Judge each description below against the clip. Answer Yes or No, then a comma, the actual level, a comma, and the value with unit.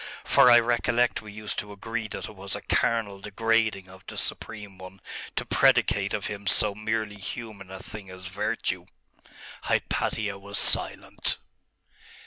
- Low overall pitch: Yes, low, 105 Hz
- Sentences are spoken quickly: No, average, 150 wpm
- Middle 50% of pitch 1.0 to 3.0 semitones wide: Yes, narrow, 2.4 semitones